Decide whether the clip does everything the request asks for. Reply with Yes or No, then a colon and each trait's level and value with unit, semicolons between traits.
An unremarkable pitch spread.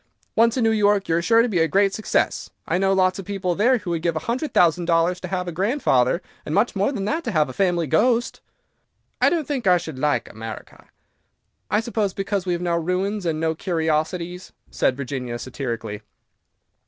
Yes: average, 4.3 semitones